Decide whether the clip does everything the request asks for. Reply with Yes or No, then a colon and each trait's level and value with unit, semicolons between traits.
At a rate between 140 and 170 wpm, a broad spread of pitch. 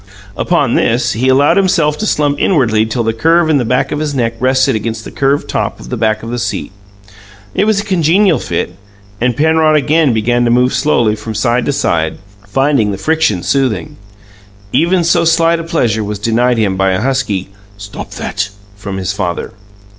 No: average, 190 wpm; wide, 6.1 semitones